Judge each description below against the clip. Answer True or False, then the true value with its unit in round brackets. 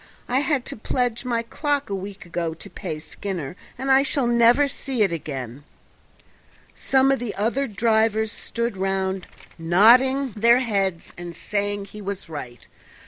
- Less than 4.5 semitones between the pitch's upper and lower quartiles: False (4.8 semitones)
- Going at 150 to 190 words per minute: True (155 wpm)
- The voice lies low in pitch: False (215 Hz)